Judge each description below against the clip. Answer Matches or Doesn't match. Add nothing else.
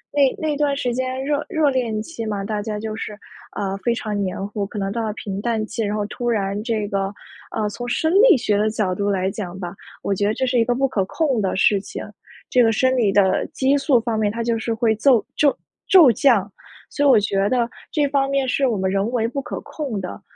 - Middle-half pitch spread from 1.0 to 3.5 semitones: Doesn't match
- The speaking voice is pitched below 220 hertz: Doesn't match